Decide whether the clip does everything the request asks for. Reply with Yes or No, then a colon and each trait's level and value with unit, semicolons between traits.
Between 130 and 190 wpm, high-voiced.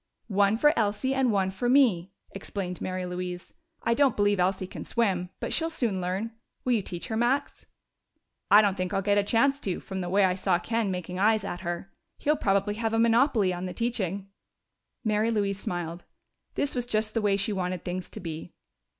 No: average, 200 wpm; high, 200 Hz